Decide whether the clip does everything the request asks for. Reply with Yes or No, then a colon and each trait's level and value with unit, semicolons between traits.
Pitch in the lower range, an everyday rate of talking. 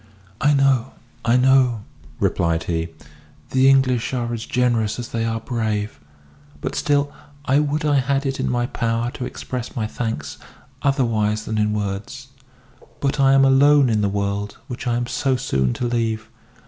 Yes: low, 120 Hz; average, 170 wpm